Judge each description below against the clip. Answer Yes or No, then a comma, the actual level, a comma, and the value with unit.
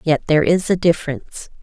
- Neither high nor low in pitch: Yes, medium, 160 Hz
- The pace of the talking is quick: No, average, 185 wpm